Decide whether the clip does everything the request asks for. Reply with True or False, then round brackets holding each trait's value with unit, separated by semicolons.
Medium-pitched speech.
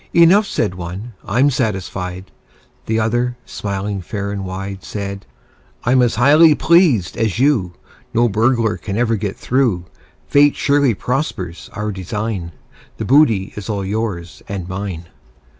False (105 Hz)